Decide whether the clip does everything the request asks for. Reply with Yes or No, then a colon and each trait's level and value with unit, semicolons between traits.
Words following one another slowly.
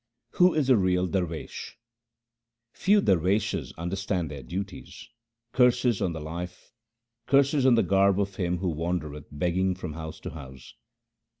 No: average, 155 wpm